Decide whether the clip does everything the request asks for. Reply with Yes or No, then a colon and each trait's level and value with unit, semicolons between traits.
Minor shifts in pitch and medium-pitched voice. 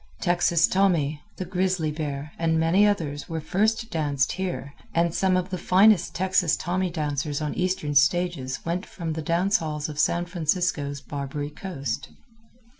No: average, 3.6 semitones; medium, 165 Hz